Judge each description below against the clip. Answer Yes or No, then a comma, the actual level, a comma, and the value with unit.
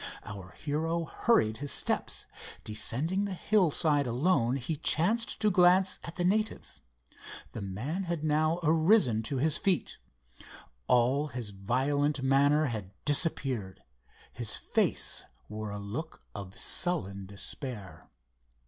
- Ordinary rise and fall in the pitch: No, wide, 7.2 semitones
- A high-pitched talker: No, medium, 145 Hz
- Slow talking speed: Yes, slow, 120 wpm